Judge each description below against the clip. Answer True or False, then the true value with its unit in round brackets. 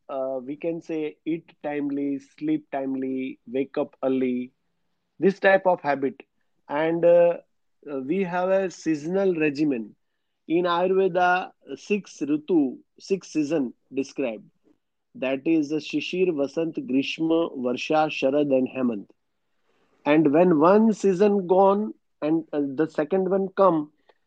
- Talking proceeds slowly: True (125 wpm)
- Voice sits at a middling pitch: True (160 Hz)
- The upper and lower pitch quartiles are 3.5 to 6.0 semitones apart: True (5.4 semitones)